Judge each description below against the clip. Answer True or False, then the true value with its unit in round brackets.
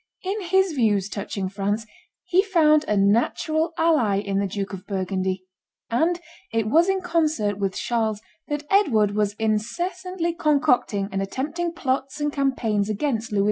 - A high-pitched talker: True (235 Hz)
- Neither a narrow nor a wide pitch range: False (8.3 semitones)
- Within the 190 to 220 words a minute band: False (155 wpm)